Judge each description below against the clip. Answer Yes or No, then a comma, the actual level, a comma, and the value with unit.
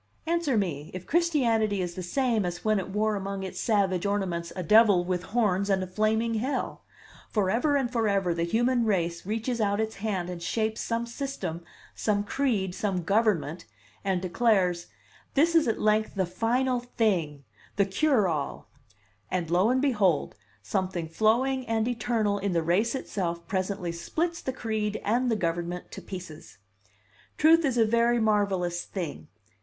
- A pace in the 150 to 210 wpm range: Yes, average, 160 wpm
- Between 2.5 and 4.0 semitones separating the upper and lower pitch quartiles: No, average, 4.4 semitones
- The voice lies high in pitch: Yes, high, 205 Hz